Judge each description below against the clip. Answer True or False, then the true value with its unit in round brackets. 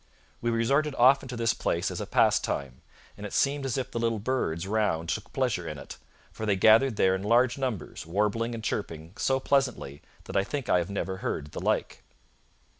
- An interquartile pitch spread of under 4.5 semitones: False (5.3 semitones)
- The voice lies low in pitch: True (110 Hz)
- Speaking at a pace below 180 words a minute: False (200 wpm)